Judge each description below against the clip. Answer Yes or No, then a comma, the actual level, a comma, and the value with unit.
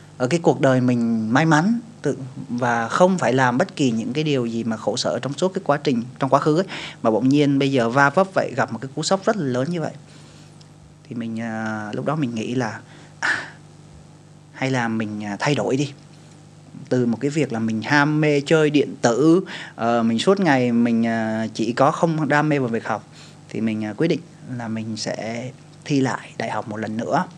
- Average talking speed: Yes, average, 215 wpm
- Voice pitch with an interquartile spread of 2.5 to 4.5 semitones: No, average, 5.0 semitones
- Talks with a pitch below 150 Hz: Yes, low, 135 Hz